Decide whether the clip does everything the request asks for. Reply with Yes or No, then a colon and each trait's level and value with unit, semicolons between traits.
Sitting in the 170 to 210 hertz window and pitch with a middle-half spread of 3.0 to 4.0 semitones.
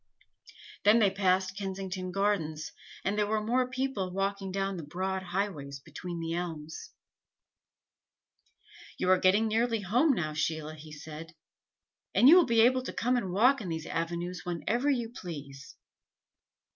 No: high, 190 Hz; average, 4.8 semitones